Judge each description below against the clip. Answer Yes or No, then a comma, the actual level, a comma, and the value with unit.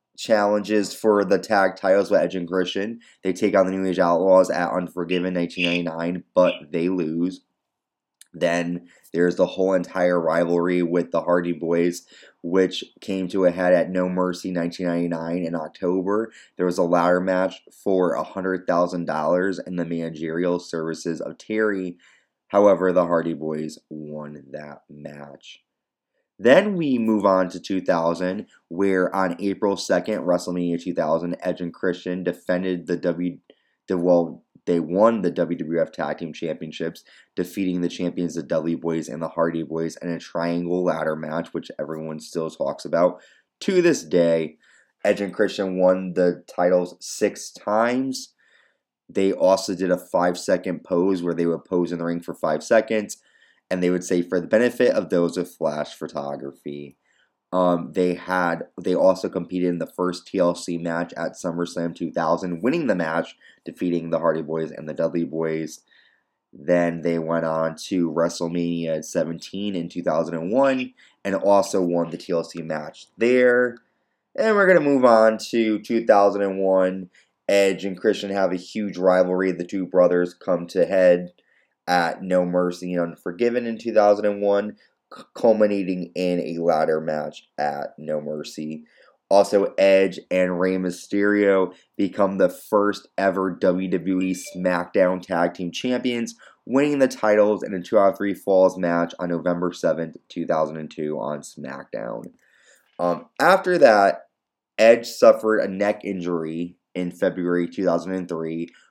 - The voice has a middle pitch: No, very low, 90 Hz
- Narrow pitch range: Yes, narrow, 2.1 semitones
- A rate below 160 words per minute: Yes, average, 150 wpm